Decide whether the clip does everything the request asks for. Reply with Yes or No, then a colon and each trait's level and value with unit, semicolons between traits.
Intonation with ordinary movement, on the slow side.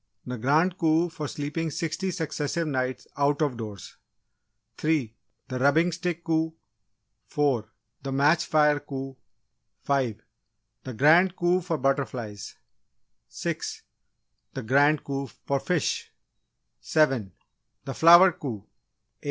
Yes: average, 3.6 semitones; slow, 120 wpm